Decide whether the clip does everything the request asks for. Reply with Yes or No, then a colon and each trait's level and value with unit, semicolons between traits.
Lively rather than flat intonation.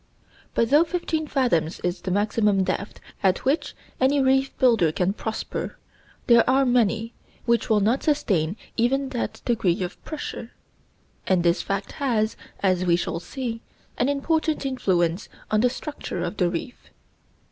Yes: wide, 6.2 semitones